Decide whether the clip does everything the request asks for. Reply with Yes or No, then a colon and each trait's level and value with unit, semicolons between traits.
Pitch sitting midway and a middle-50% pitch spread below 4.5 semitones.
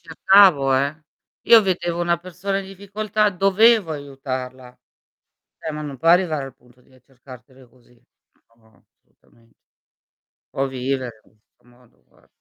No: medium, 145 Hz; wide, 6.3 semitones